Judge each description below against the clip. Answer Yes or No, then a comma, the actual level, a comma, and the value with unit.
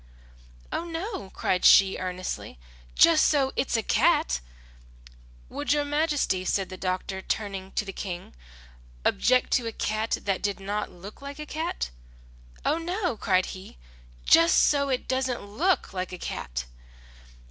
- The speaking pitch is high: Yes, high, 210 Hz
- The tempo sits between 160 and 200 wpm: No, average, 150 wpm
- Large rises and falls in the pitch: Yes, wide, 7.6 semitones